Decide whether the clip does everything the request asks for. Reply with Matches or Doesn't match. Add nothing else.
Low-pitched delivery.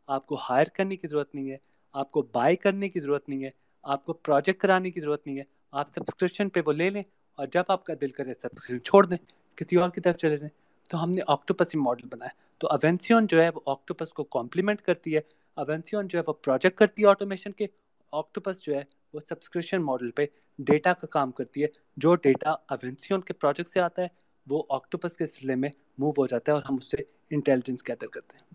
Doesn't match